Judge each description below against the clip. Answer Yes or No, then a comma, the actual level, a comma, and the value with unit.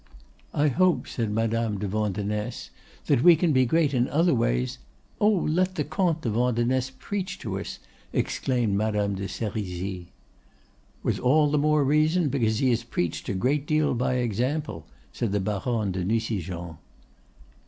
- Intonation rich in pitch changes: Yes, wide, 6.3 semitones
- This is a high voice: No, low, 120 Hz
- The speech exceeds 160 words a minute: No, average, 155 wpm